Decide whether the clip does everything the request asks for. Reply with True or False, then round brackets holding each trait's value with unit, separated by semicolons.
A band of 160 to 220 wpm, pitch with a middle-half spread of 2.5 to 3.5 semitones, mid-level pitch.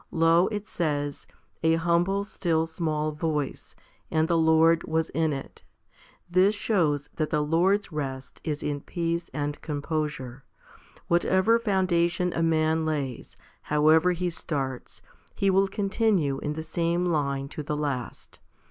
False (145 wpm; 2.9 semitones; 160 Hz)